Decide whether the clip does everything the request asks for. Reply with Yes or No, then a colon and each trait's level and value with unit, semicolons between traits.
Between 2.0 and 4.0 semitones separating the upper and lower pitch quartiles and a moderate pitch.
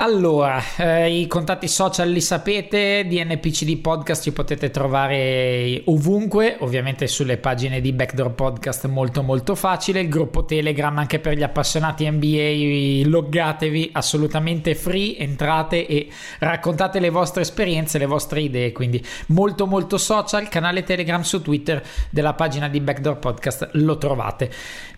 Yes: average, 3.5 semitones; medium, 155 Hz